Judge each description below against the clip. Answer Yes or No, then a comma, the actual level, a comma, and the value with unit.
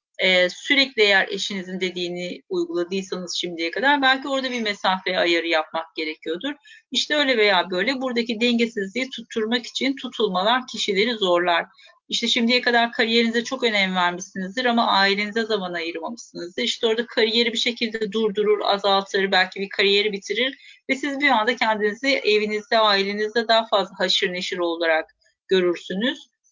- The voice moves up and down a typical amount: Yes, average, 4.5 semitones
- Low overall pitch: No, high, 215 Hz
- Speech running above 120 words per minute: Yes, fast, 140 wpm